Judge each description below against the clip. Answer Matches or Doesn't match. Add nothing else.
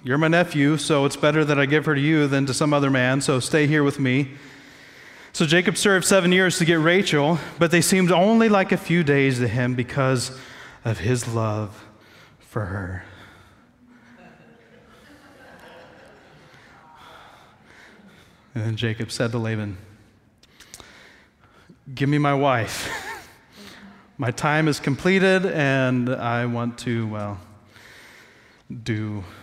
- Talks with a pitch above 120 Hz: Matches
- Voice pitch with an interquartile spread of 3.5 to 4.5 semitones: Doesn't match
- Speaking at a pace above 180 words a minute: Doesn't match